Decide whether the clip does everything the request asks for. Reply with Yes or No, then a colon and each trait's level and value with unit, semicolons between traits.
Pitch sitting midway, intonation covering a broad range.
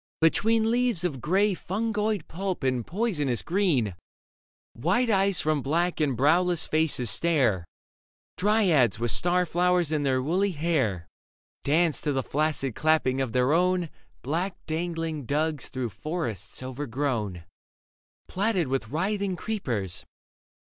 Yes: medium, 155 Hz; wide, 5.7 semitones